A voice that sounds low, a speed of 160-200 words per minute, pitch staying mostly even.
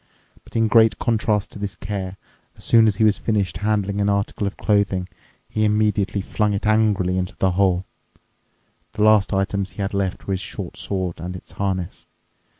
Yes: low, 100 Hz; average, 180 wpm; narrow, 2.0 semitones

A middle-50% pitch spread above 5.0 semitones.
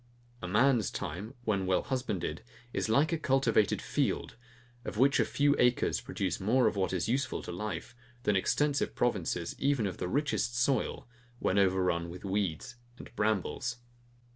Yes: wide, 5.6 semitones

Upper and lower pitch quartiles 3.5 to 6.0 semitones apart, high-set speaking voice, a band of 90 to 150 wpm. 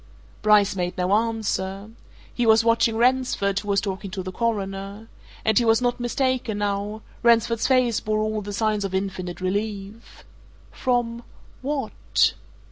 No: average, 2.7 semitones; high, 215 Hz; average, 145 wpm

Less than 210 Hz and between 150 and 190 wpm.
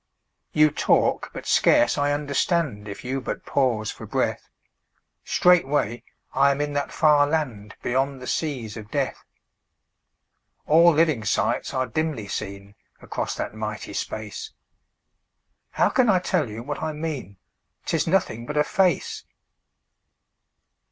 No: medium, 140 Hz; slow, 135 wpm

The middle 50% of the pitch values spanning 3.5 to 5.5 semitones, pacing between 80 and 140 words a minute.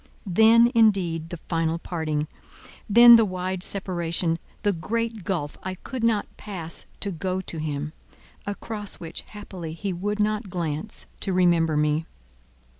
Yes: average, 4.1 semitones; slow, 135 wpm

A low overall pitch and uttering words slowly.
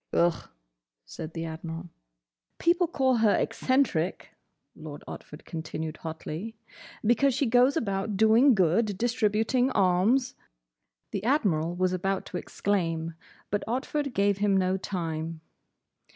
No: high, 195 Hz; slow, 115 wpm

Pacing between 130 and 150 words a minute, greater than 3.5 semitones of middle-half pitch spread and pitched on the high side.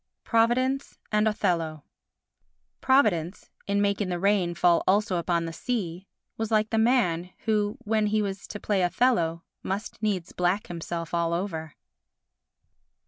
Yes: average, 140 wpm; average, 3.9 semitones; high, 195 Hz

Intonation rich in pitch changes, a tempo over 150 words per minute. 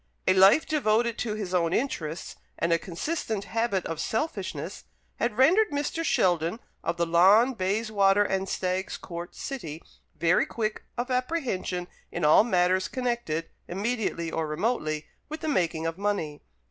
No: wide, 5.7 semitones; average, 145 wpm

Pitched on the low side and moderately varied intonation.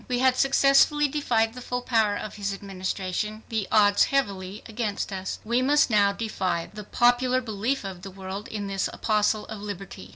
No: high, 215 Hz; average, 3.8 semitones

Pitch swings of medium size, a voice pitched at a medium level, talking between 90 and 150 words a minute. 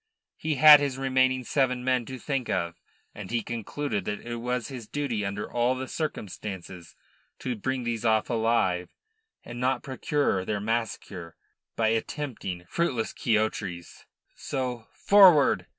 No: average, 3.9 semitones; low, 120 Hz; average, 140 wpm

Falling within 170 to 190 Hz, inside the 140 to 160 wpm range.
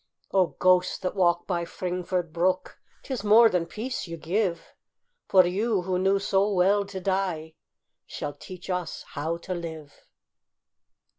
Yes: medium, 185 Hz; average, 145 wpm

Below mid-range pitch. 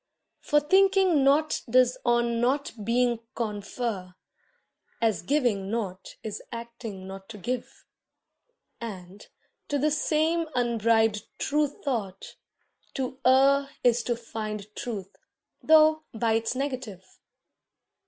No: high, 235 Hz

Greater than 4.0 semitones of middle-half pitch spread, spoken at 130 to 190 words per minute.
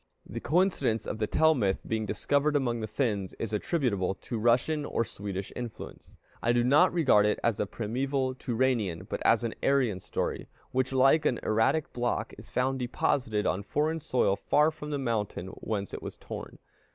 Yes: average, 4.5 semitones; average, 180 wpm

